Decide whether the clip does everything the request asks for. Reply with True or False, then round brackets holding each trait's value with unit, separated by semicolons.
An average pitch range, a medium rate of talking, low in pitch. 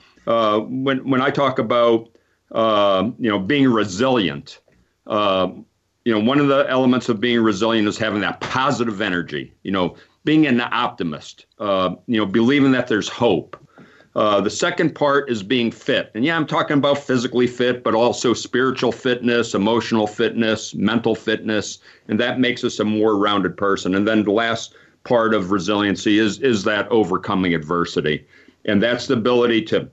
True (3.3 semitones; 170 wpm; 115 Hz)